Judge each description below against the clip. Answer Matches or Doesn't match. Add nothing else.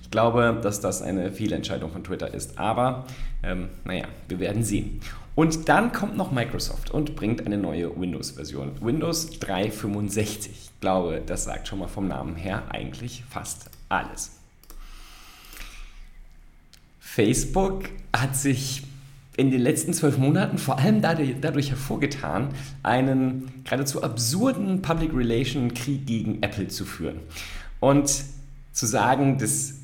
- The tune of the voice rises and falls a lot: Matches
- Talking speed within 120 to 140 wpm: Matches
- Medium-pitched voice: Doesn't match